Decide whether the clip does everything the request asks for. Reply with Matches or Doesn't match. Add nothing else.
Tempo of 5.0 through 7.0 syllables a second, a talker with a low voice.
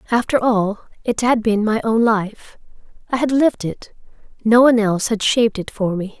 Doesn't match